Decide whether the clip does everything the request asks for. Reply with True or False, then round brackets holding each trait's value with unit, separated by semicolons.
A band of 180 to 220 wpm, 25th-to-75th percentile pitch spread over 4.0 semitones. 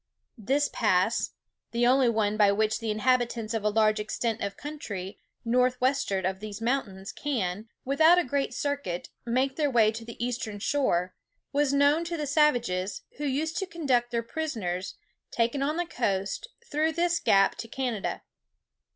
False (165 wpm; 5.1 semitones)